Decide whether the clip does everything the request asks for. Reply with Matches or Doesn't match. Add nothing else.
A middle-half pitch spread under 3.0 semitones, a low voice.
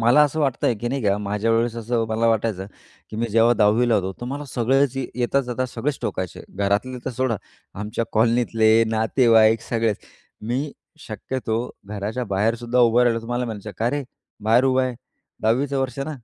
Matches